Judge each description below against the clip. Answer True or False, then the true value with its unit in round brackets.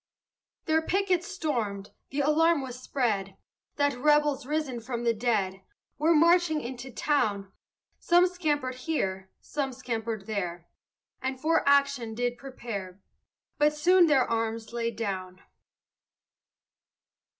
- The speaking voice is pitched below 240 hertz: False (255 Hz)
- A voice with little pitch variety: False (5.3 semitones)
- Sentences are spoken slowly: True (120 wpm)